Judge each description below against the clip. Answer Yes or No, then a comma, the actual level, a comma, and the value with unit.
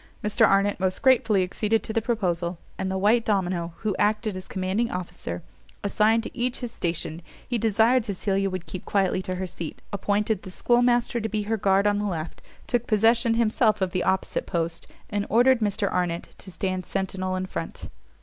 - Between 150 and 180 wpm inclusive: No, average, 190 wpm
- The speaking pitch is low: No, high, 200 Hz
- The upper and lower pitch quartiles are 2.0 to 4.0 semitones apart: Yes, average, 3.3 semitones